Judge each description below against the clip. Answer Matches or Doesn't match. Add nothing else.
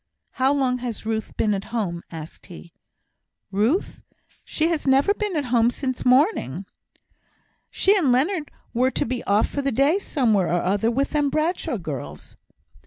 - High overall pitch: Matches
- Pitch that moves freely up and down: Matches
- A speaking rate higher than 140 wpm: Matches